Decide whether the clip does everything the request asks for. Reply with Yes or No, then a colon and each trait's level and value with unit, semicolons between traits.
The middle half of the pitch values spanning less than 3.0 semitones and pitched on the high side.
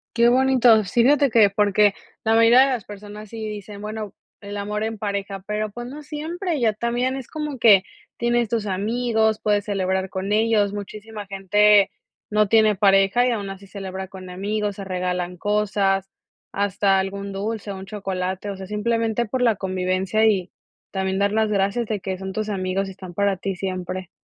Yes: narrow, 2.5 semitones; high, 205 Hz